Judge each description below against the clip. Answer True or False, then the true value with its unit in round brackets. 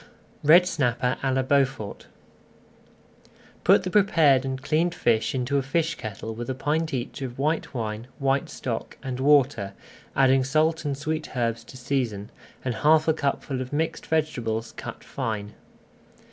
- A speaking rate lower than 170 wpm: True (155 wpm)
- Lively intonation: False (4.1 semitones)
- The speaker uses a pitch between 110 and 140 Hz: True (135 Hz)